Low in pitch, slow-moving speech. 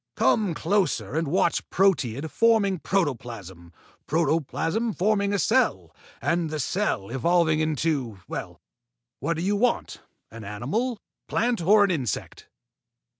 No: medium, 165 Hz; slow, 125 wpm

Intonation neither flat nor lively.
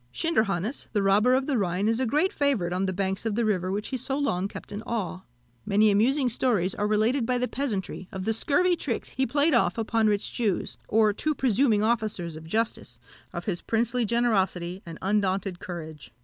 Yes: average, 4.5 semitones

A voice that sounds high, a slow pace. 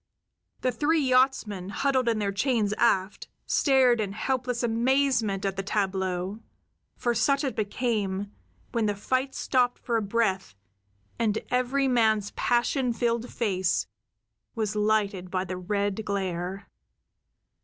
Yes: high, 220 Hz; slow, 130 wpm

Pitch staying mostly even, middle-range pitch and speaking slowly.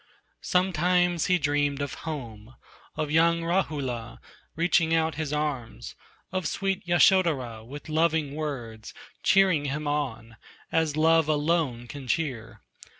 No: average, 4.1 semitones; medium, 150 Hz; slow, 120 wpm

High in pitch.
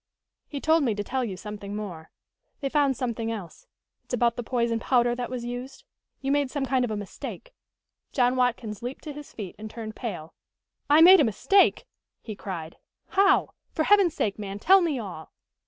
Yes: high, 245 Hz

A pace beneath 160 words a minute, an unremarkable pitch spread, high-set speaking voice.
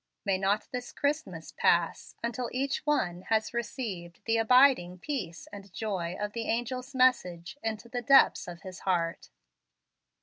No: average, 145 wpm; wide, 5.8 semitones; high, 220 Hz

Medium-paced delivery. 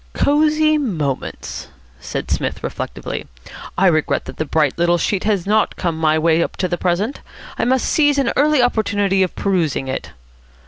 Yes: average, 170 wpm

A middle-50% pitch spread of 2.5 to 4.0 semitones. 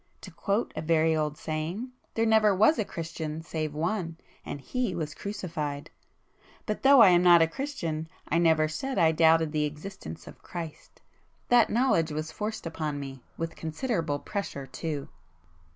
No: average, 4.6 semitones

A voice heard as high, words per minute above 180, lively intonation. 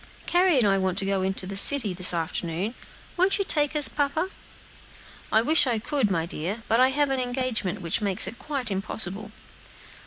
Yes: high, 220 Hz; average, 190 wpm; wide, 6.7 semitones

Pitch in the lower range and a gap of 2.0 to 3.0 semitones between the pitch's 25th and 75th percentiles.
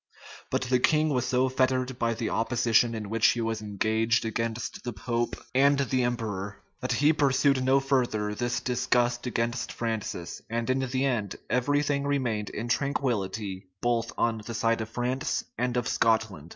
Yes: low, 120 Hz; narrow, 2.5 semitones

